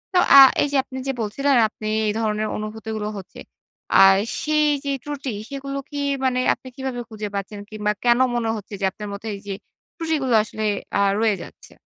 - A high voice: Yes, high, 225 Hz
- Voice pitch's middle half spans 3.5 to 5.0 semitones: Yes, average, 4.5 semitones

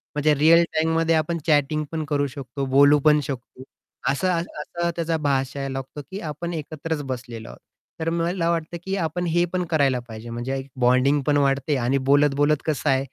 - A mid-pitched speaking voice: Yes, medium, 150 Hz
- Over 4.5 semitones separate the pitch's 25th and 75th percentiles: No, average, 3.2 semitones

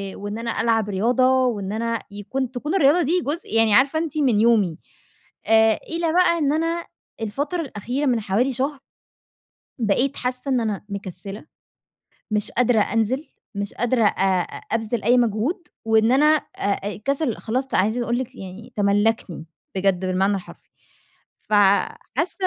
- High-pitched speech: Yes, high, 230 Hz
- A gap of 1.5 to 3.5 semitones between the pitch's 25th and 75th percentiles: No, average, 4.7 semitones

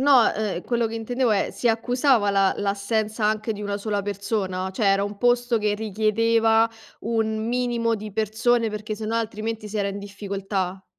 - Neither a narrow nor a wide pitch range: No, narrow, 2.1 semitones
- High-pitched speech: Yes, high, 215 Hz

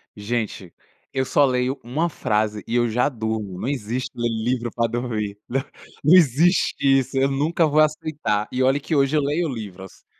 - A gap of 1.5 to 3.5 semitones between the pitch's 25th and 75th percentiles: No, average, 4.5 semitones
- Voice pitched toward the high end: No, low, 125 Hz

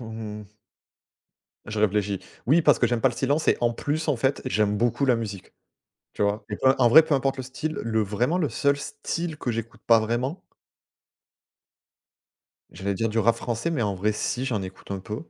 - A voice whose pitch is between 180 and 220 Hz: No, low, 115 Hz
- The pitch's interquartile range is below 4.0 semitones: No, average, 4.5 semitones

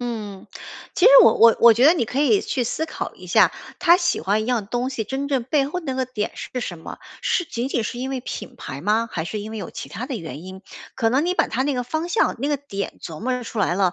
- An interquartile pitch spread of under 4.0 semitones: No, average, 4.7 semitones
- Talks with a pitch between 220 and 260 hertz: Yes, high, 245 Hz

